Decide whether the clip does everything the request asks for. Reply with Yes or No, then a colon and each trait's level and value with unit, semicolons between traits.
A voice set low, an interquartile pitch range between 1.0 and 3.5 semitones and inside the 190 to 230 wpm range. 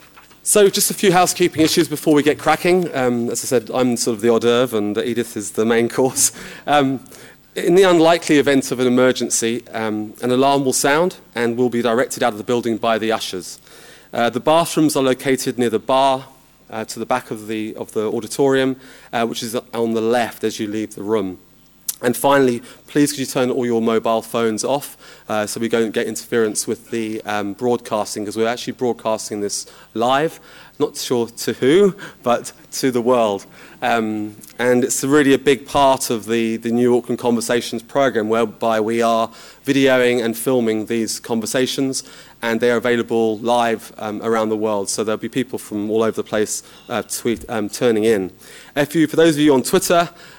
Yes: low, 120 Hz; average, 3.2 semitones; average, 195 wpm